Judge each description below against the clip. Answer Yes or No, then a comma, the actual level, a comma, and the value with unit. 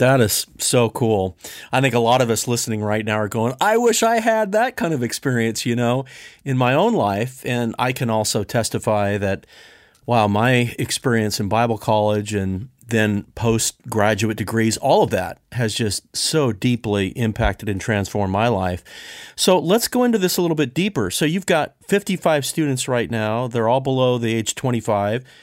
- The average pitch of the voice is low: Yes, low, 115 Hz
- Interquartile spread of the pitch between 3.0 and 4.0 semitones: Yes, average, 3.4 semitones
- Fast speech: No, average, 185 wpm